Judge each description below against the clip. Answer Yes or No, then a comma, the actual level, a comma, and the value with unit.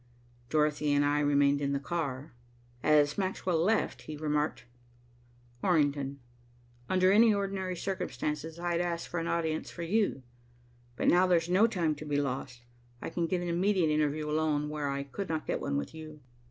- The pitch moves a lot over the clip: No, average, 3.4 semitones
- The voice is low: No, medium, 155 Hz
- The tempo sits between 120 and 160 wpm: No, average, 170 wpm